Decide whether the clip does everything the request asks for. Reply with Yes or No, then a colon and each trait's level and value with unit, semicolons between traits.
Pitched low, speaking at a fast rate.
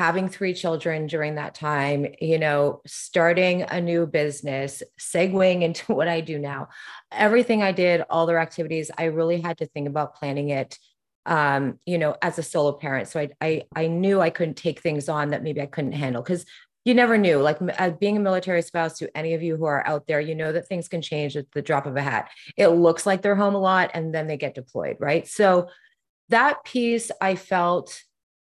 No: medium, 165 Hz; fast, 215 wpm